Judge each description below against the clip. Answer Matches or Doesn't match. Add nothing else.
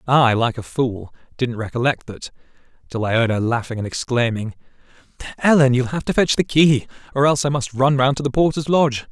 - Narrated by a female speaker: Doesn't match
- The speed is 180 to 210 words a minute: Matches